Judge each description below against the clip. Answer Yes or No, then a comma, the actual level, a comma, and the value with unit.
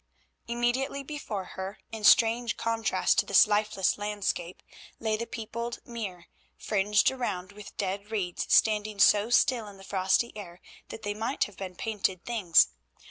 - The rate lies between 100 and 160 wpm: Yes, average, 150 wpm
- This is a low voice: No, high, 210 Hz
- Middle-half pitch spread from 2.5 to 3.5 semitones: Yes, average, 3.0 semitones